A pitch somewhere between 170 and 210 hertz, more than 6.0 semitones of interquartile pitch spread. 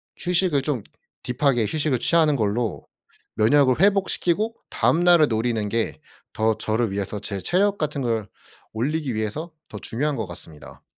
No: low, 125 Hz; wide, 6.4 semitones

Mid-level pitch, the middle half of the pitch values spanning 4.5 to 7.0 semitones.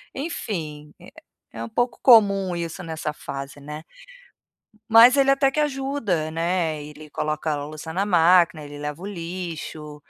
Yes: medium, 165 Hz; average, 5.2 semitones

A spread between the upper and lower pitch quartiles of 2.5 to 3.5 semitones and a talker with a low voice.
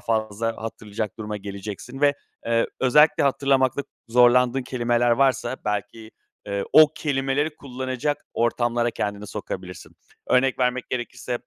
Yes: average, 2.9 semitones; low, 120 Hz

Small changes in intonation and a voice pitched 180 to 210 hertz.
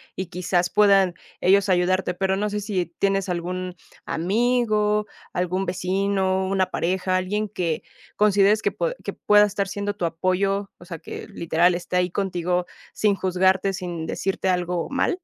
Yes: narrow, 2.0 semitones; high, 190 Hz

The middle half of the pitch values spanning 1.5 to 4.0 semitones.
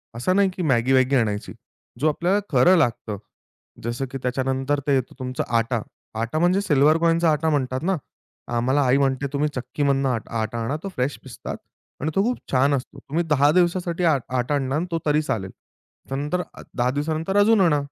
No: average, 4.4 semitones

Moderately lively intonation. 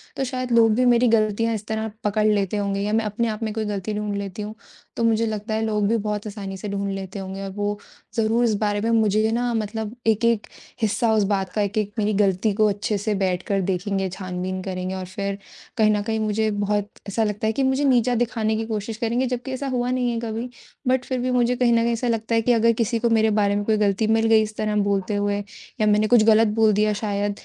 No: narrow, 2.1 semitones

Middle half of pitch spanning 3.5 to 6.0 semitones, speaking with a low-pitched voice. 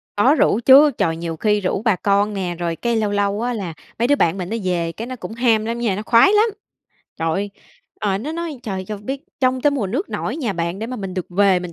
No: average, 4.8 semitones; high, 210 Hz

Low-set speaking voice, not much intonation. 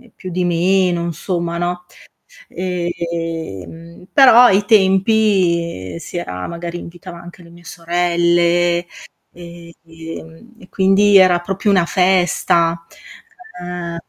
No: medium, 175 Hz; narrow, 1.7 semitones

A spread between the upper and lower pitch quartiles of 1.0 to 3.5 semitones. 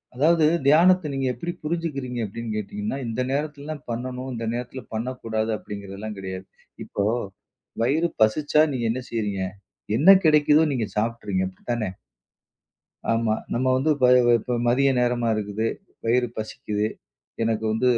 No: average, 4.5 semitones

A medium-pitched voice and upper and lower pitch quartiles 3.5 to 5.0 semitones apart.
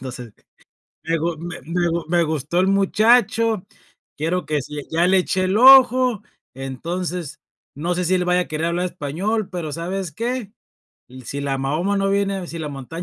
Yes: medium, 175 Hz; average, 4.0 semitones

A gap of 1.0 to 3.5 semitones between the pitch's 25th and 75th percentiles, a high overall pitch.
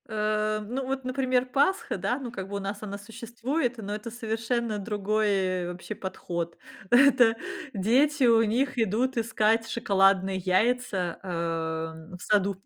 No: average, 4.0 semitones; high, 215 Hz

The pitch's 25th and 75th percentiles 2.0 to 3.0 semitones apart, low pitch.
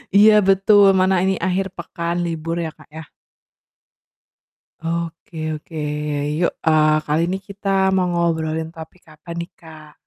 No: narrow, 2.6 semitones; medium, 170 Hz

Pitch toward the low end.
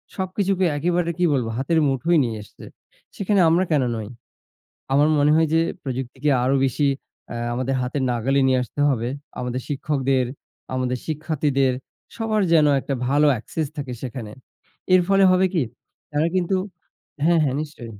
No: medium, 145 Hz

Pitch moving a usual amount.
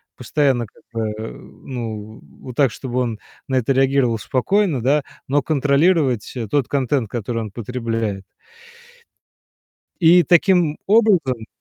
Yes: average, 4.4 semitones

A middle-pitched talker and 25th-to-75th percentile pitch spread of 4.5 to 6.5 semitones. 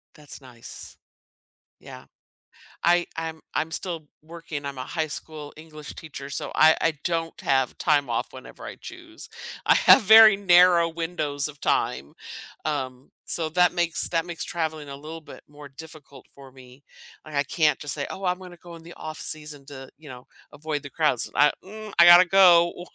No: medium, 155 Hz; average, 3.3 semitones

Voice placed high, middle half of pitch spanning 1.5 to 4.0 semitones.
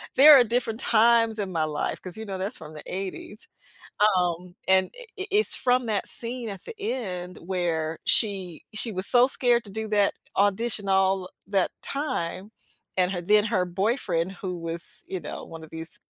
No: high, 195 Hz; average, 4.5 semitones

